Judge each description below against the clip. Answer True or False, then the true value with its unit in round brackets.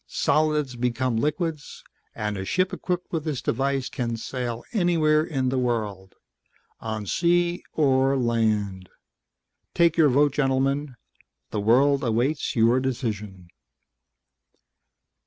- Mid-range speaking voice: False (130 Hz)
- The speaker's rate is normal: False (115 wpm)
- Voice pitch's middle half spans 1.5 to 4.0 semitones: False (4.9 semitones)